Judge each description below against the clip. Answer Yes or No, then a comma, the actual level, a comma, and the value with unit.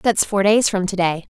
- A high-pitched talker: Yes, high, 195 Hz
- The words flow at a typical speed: No, fast, 225 wpm